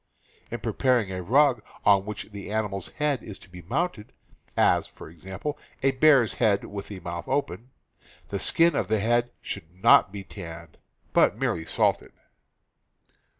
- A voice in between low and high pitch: No, low, 105 Hz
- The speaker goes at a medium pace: Yes, average, 165 wpm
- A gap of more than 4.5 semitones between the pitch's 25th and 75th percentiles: Yes, average, 5.1 semitones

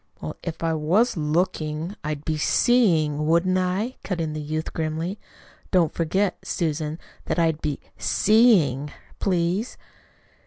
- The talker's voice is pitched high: No, medium, 165 Hz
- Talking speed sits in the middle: No, slow, 130 wpm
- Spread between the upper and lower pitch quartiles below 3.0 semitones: No, average, 3.4 semitones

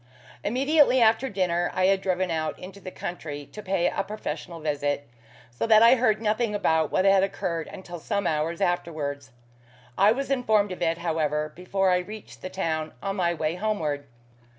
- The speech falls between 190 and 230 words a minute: No, average, 175 wpm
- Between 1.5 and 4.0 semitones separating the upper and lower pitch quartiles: No, average, 4.6 semitones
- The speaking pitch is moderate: Yes, medium, 180 Hz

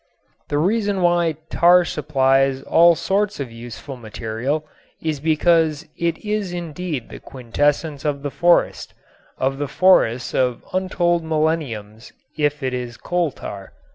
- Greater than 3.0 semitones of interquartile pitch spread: Yes, average, 4.7 semitones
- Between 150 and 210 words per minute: No, slow, 135 wpm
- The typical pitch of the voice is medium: Yes, medium, 150 Hz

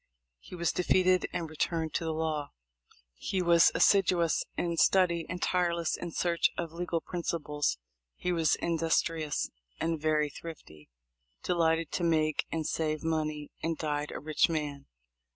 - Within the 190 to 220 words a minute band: No, average, 150 wpm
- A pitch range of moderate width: No, narrow, 1.7 semitones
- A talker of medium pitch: Yes, medium, 165 Hz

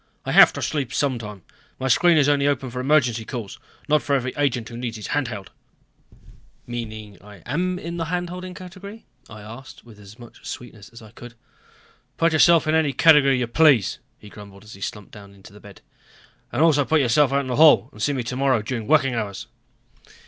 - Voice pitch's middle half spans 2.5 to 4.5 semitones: No, wide, 5.5 semitones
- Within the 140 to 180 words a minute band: No, fast, 205 wpm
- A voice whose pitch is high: No, low, 125 Hz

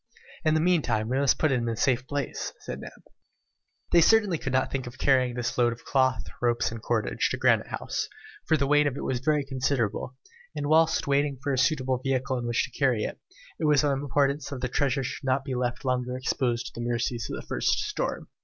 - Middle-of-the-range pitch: No, low, 130 Hz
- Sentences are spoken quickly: Yes, fast, 230 wpm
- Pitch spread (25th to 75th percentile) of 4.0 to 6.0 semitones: No, narrow, 2.6 semitones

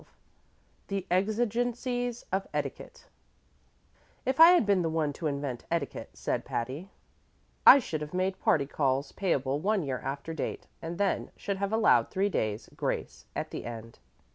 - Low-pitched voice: No, medium, 180 Hz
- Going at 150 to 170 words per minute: Yes, average, 160 wpm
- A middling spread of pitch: No, wide, 6.8 semitones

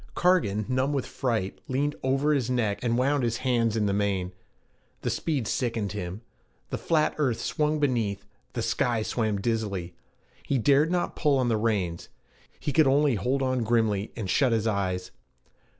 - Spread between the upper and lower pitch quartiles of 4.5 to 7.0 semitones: Yes, average, 4.8 semitones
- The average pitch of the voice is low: Yes, low, 120 Hz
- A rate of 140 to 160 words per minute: No, average, 170 wpm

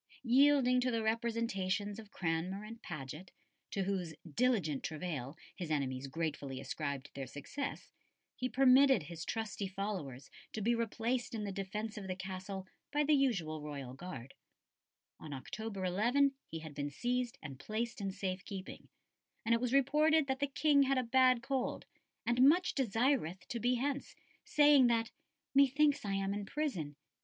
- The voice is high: Yes, high, 210 Hz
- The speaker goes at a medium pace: Yes, average, 160 wpm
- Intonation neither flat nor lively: No, wide, 7.2 semitones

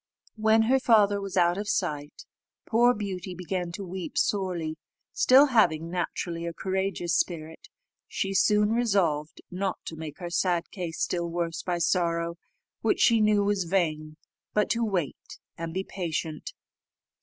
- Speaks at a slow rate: No, average, 150 wpm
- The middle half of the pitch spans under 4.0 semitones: Yes, average, 3.4 semitones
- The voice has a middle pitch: Yes, medium, 180 Hz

